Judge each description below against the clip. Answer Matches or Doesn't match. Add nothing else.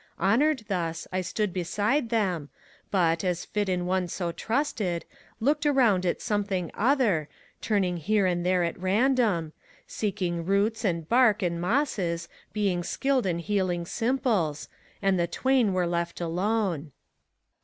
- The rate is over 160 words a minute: Doesn't match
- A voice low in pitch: Doesn't match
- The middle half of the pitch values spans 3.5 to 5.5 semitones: Matches